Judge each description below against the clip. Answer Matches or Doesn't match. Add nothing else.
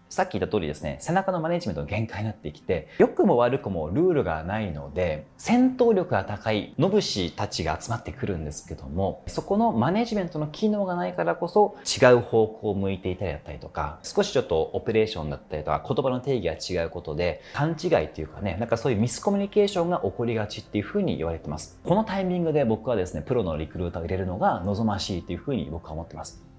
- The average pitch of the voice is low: Matches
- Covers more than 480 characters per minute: Matches